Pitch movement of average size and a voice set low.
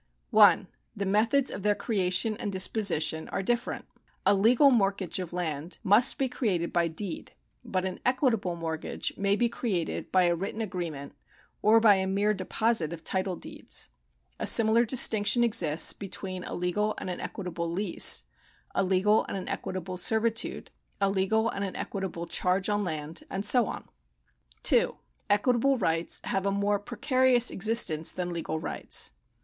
No: average, 3.6 semitones; high, 195 Hz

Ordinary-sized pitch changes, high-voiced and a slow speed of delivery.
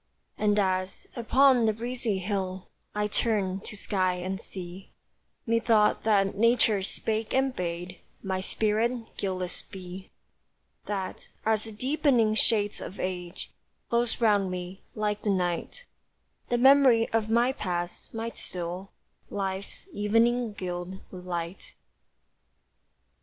Yes: average, 3.5 semitones; high, 205 Hz; slow, 120 wpm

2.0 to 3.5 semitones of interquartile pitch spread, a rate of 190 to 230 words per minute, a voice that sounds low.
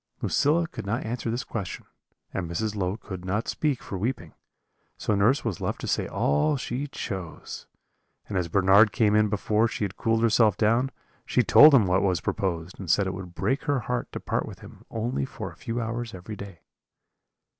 No: average, 4.0 semitones; average, 200 wpm; low, 105 Hz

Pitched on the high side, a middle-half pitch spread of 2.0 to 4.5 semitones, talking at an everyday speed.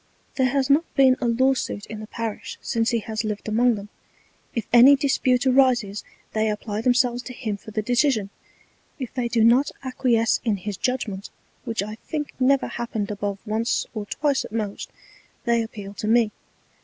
Yes: high, 230 Hz; average, 3.2 semitones; average, 180 wpm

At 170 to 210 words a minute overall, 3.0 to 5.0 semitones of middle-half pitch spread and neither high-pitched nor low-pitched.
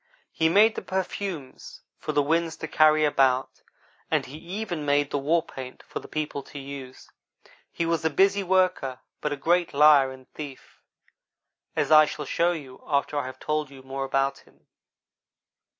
Yes: average, 175 wpm; average, 3.6 semitones; medium, 150 Hz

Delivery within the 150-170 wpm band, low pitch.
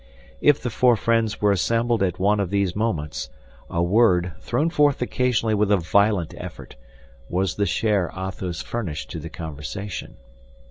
Yes: average, 155 wpm; low, 100 Hz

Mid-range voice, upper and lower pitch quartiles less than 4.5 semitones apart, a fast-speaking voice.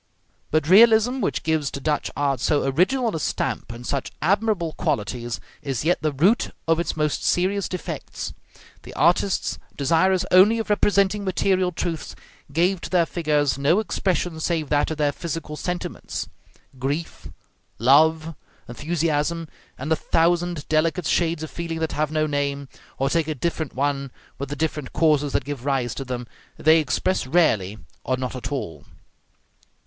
No: medium, 155 Hz; average, 3.8 semitones; average, 160 wpm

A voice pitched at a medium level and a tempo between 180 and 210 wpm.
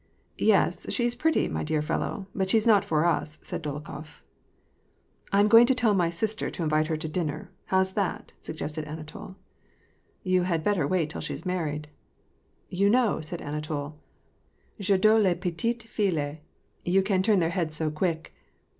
Yes: medium, 175 Hz; average, 185 wpm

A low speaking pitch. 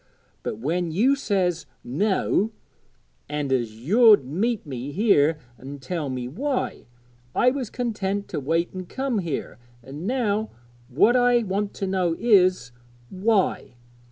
No: medium, 185 Hz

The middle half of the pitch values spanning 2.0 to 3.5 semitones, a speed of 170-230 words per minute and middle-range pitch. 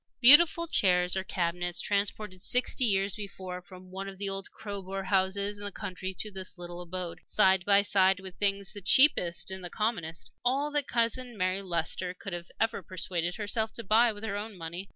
No: narrow, 2.5 semitones; average, 190 wpm; high, 195 Hz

